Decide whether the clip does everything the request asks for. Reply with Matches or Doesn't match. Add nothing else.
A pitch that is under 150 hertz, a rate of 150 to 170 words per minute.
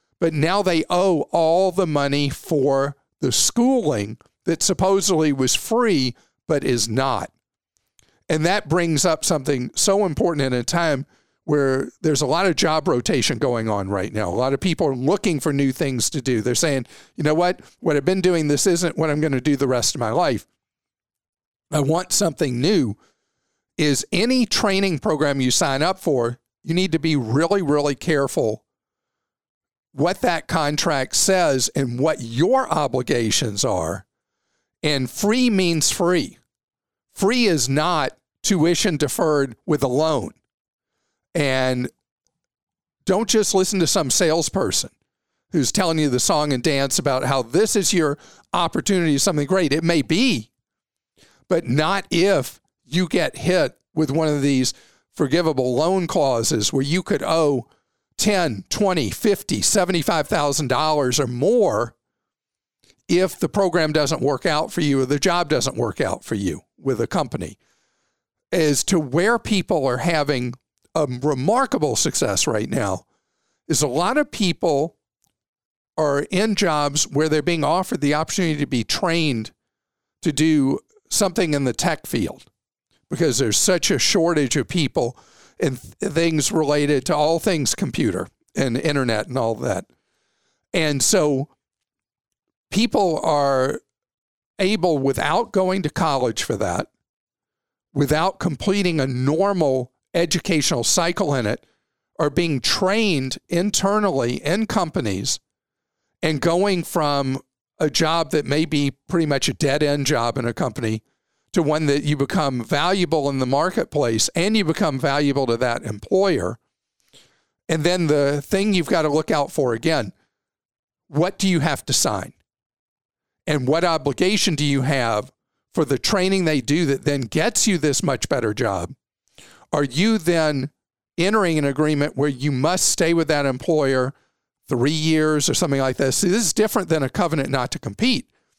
Doesn't match